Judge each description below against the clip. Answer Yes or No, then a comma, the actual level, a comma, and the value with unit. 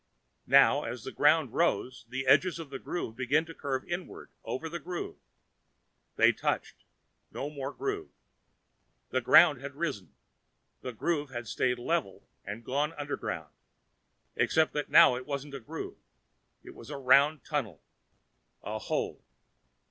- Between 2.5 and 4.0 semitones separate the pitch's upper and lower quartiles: Yes, average, 3.7 semitones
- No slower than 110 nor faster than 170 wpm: Yes, average, 145 wpm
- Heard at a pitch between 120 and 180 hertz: Yes, medium, 140 Hz